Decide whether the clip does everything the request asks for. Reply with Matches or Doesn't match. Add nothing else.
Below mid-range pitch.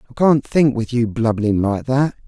Matches